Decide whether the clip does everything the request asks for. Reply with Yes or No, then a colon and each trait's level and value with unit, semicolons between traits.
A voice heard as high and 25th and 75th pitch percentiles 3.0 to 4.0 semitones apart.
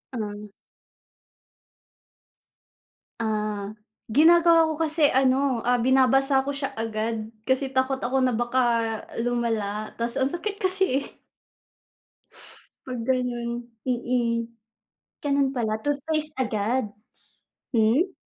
Yes: very high, 255 Hz; average, 3.6 semitones